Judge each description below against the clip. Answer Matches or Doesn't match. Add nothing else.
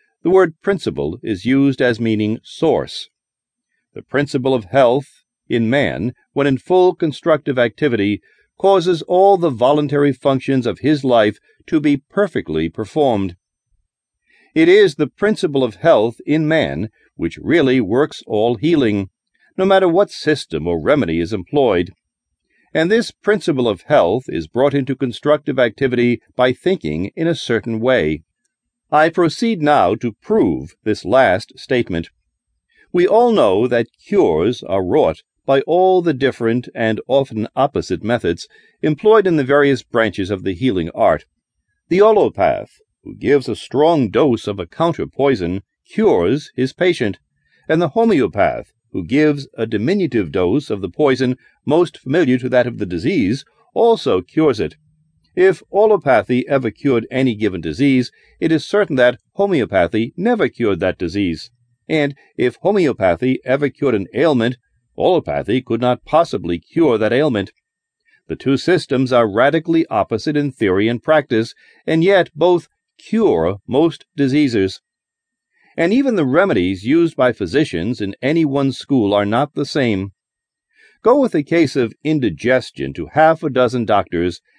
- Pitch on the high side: Doesn't match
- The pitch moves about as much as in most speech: Doesn't match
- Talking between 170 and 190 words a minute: Doesn't match